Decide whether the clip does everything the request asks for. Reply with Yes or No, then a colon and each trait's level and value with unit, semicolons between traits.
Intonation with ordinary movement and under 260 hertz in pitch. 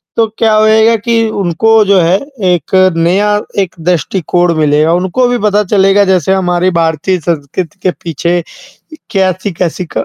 Yes: average, 3.1 semitones; medium, 185 Hz